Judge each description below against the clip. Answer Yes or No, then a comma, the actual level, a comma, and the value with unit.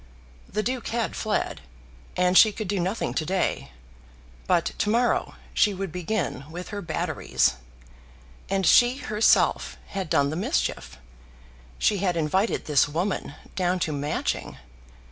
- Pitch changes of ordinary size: Yes, average, 4.3 semitones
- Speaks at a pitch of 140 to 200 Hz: Yes, high, 190 Hz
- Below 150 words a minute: Yes, average, 140 wpm